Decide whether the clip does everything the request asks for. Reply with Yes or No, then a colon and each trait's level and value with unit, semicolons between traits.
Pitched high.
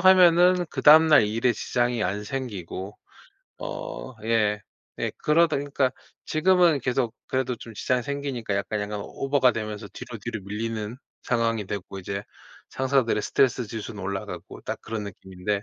No: low, 115 Hz